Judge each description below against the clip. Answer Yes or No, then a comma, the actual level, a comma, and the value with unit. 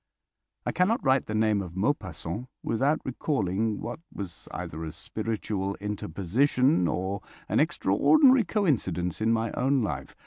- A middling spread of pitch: No, wide, 6.0 semitones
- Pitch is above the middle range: No, low, 110 Hz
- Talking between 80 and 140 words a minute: Yes, slow, 135 wpm